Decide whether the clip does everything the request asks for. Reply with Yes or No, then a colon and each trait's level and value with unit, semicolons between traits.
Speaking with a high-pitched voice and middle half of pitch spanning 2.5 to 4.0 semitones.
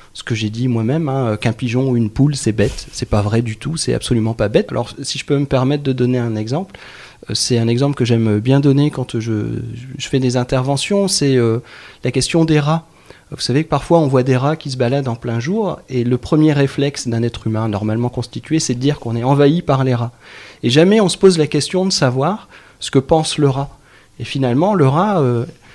No: low, 130 Hz; average, 3.7 semitones